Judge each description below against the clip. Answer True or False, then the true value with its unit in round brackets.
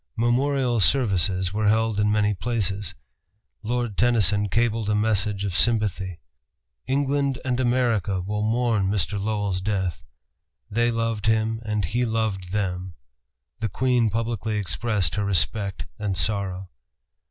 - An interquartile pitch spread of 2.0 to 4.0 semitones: True (3.1 semitones)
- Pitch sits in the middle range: False (105 Hz)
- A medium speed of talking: False (130 wpm)